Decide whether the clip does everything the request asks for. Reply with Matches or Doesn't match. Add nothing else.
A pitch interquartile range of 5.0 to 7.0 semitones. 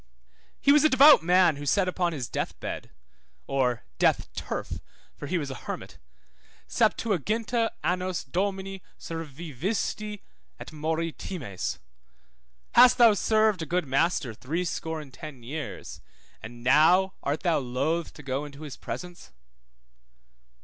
Matches